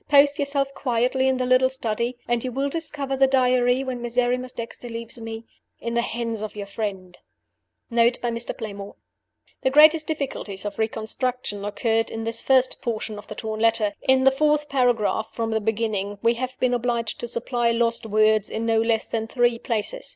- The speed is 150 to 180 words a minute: No, average, 190 wpm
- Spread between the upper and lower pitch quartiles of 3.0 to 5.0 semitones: No, narrow, 2.6 semitones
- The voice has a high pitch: Yes, high, 235 Hz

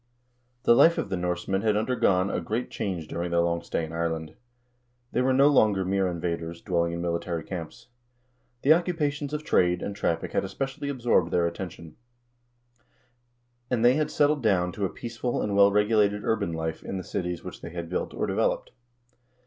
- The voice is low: Yes, very low, 95 Hz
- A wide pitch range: Yes, wide, 5.8 semitones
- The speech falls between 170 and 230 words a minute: Yes, average, 185 wpm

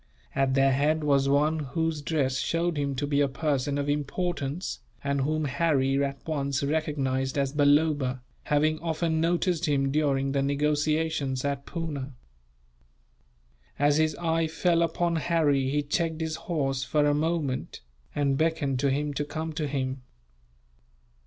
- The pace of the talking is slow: No, average, 150 wpm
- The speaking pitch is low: No, medium, 145 Hz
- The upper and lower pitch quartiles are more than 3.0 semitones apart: No, narrow, 2.5 semitones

